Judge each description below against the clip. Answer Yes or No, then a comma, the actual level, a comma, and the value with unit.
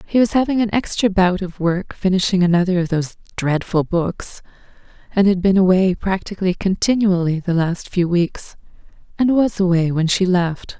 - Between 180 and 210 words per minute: No, average, 165 wpm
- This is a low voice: No, medium, 185 Hz